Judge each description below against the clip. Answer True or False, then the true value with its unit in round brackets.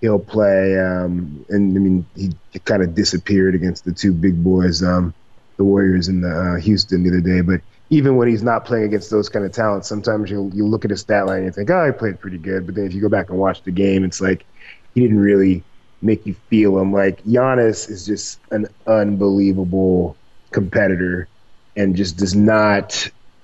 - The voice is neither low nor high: False (100 Hz)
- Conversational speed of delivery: False (210 wpm)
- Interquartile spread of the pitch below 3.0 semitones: True (2.4 semitones)